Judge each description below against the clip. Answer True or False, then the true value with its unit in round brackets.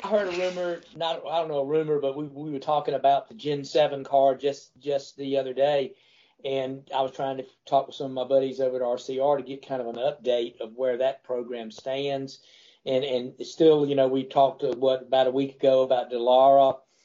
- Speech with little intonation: True (1.9 semitones)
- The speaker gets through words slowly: False (220 wpm)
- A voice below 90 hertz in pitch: False (135 Hz)